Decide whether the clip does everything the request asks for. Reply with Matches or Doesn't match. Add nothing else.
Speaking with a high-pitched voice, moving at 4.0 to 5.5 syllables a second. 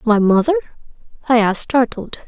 Doesn't match